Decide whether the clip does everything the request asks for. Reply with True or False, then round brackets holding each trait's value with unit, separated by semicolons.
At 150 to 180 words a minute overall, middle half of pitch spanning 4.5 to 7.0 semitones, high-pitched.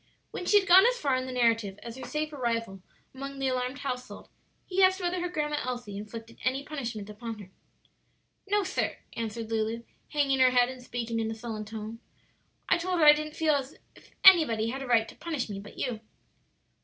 False (205 wpm; 5.0 semitones; 255 Hz)